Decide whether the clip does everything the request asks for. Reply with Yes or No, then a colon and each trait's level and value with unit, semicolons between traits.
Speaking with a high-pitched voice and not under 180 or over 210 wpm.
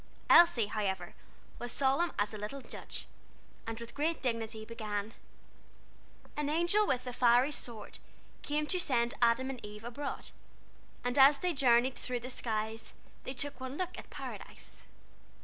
No: high, 245 Hz; average, 150 wpm